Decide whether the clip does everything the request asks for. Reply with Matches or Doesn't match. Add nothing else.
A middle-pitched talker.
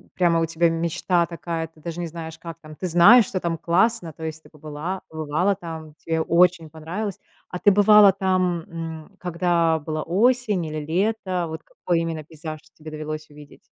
Matches